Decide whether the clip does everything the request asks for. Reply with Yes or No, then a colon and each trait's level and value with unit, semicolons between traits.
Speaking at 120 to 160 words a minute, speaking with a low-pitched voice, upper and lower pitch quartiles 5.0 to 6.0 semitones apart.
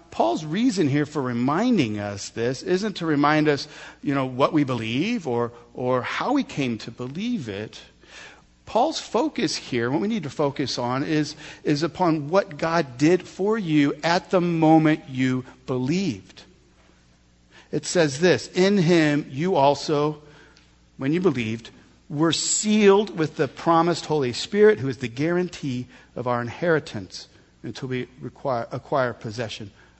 No: average, 150 wpm; medium, 145 Hz; average, 5.3 semitones